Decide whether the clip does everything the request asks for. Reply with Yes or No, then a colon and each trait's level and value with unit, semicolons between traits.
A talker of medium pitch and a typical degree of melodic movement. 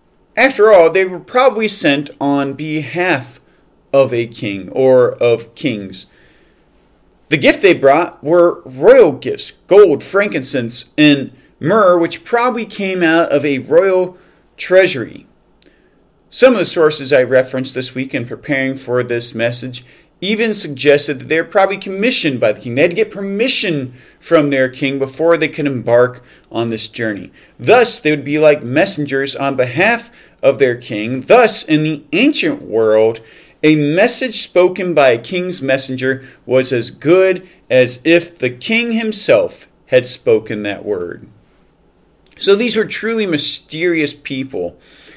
No: medium, 155 Hz; wide, 7.3 semitones